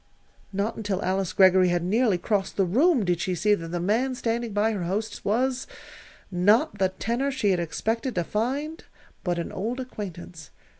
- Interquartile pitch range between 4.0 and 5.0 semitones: Yes, average, 4.5 semitones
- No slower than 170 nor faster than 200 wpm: Yes, average, 180 wpm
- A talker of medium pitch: No, high, 205 Hz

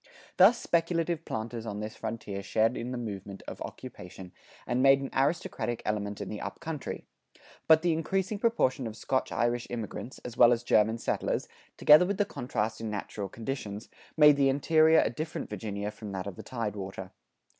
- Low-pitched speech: Yes, low, 120 Hz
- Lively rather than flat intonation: Yes, wide, 6.3 semitones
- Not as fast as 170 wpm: No, average, 180 wpm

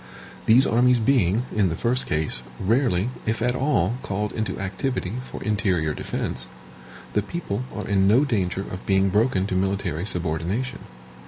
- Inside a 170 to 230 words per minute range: No, average, 155 wpm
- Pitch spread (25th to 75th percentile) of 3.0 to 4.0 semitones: No, average, 4.6 semitones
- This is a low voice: Yes, low, 105 Hz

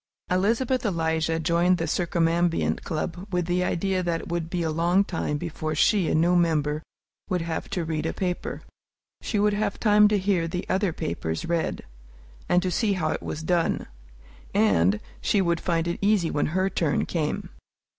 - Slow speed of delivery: No, average, 180 wpm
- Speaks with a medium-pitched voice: Yes, medium, 170 Hz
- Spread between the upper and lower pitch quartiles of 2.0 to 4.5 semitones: Yes, narrow, 2.5 semitones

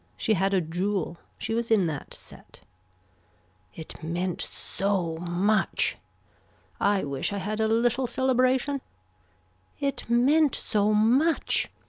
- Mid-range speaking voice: No, high, 210 Hz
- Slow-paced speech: Yes, slow, 120 wpm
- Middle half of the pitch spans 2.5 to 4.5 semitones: No, average, 5.2 semitones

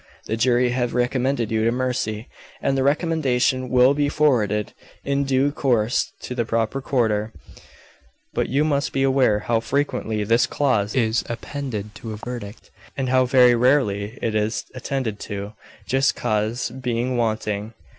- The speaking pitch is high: No, low, 125 Hz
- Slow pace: No, average, 155 wpm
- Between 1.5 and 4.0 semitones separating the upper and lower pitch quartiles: Yes, average, 3.3 semitones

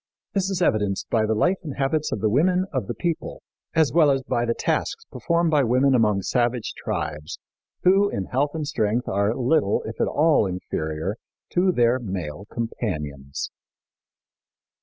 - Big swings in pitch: Yes, wide, 7.7 semitones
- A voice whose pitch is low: Yes, low, 120 Hz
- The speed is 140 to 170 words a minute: Yes, average, 165 wpm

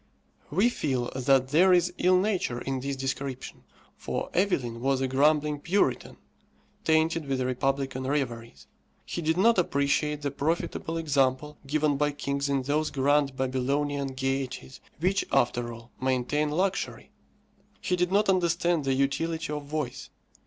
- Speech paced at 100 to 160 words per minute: Yes, average, 140 wpm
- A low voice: No, medium, 145 Hz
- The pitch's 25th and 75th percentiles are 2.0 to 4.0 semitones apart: Yes, average, 3.6 semitones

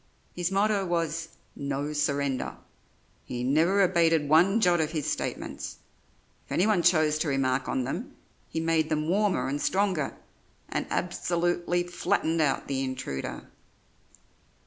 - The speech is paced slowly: Yes, slow, 130 wpm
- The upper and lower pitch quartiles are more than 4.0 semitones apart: No, average, 3.7 semitones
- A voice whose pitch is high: No, medium, 165 Hz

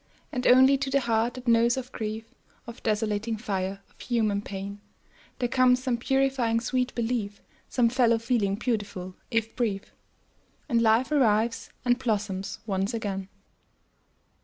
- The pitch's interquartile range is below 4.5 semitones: Yes, average, 3.3 semitones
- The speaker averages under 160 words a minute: Yes, average, 140 wpm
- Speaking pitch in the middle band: No, high, 230 Hz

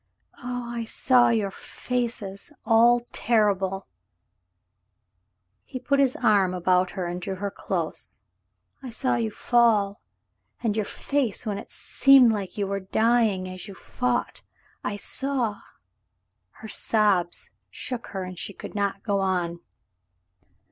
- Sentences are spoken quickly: No, average, 150 wpm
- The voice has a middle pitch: No, high, 205 Hz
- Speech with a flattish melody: No, average, 4.3 semitones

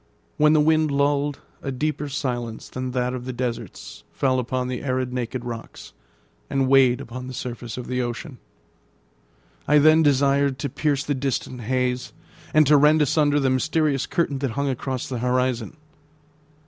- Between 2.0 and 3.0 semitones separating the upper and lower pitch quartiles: Yes, narrow, 2.4 semitones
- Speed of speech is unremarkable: Yes, average, 165 wpm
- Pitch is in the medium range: No, low, 130 Hz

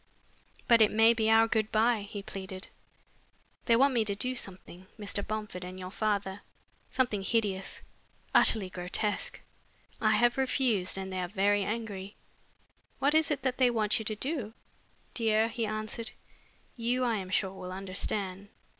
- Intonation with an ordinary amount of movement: Yes, average, 3.1 semitones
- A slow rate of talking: No, average, 160 wpm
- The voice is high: Yes, high, 215 Hz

